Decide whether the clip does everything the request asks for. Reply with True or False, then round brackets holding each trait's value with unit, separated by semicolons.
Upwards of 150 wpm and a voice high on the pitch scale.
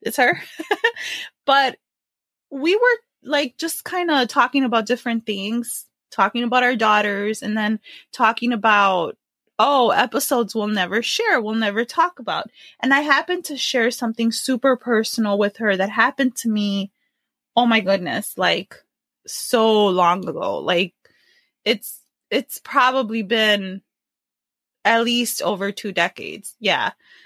False (135 wpm; 235 Hz)